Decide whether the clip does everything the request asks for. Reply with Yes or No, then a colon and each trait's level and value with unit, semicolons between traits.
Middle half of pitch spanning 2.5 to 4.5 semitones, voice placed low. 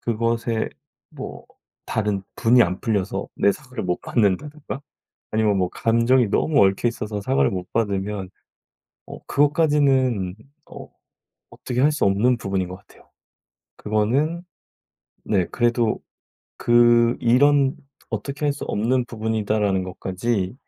Yes: average, 4.1 semitones; low, 115 Hz